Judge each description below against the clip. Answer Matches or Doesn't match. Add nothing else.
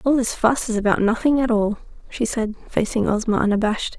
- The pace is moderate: Matches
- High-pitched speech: Matches